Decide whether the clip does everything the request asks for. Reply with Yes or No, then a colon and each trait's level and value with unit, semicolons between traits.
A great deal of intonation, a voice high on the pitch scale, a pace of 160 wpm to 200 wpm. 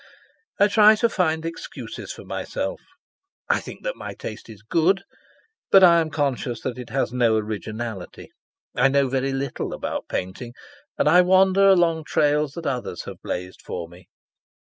No: wide, 7.1 semitones; medium, 140 Hz; average, 165 wpm